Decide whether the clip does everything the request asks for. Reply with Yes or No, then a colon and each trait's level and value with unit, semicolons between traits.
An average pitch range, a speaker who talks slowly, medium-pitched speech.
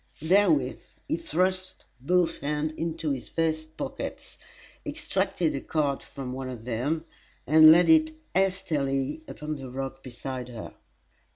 Yes: average, 3.9 semitones; slow, 130 wpm; medium, 155 Hz